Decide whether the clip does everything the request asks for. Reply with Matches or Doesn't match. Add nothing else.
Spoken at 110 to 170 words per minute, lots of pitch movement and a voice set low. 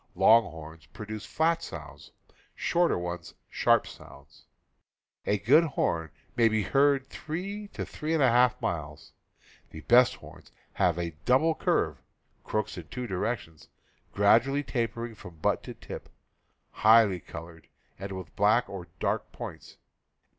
Matches